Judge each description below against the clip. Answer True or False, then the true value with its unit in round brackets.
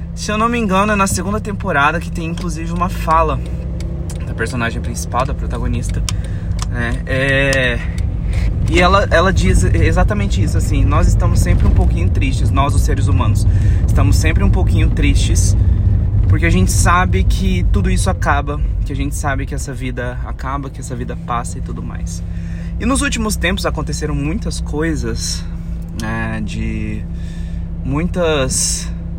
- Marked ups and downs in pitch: False (2.9 semitones)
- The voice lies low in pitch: True (95 Hz)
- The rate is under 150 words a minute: False (155 wpm)